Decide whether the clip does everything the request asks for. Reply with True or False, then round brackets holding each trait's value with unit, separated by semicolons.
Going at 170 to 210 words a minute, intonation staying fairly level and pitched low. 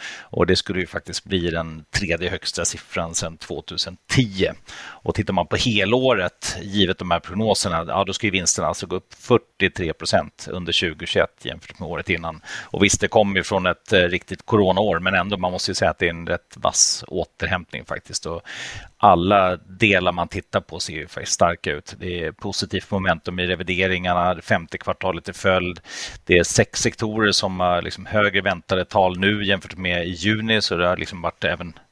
True (190 wpm; 2.2 semitones; 95 Hz)